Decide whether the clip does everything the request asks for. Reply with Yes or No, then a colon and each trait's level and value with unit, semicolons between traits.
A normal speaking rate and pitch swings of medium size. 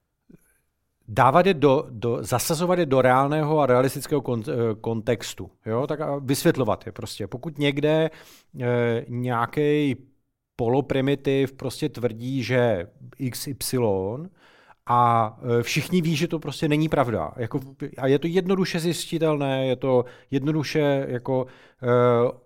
Yes: average, 125 wpm; average, 3.7 semitones